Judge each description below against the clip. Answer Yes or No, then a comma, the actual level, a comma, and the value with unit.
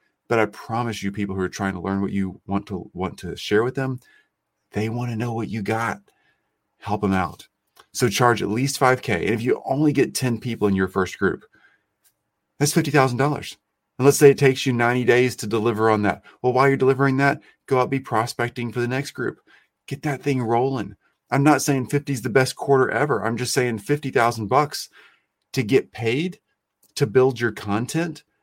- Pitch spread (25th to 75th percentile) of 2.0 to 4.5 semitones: Yes, average, 4.0 semitones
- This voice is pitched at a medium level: No, low, 125 Hz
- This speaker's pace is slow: No, fast, 205 wpm